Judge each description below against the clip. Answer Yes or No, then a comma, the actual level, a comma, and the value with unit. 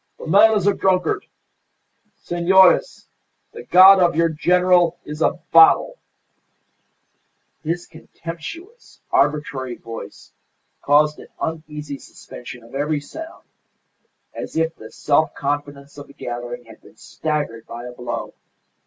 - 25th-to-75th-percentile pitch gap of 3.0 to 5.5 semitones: Yes, average, 4.3 semitones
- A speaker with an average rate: No, slow, 125 wpm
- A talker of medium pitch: Yes, medium, 155 Hz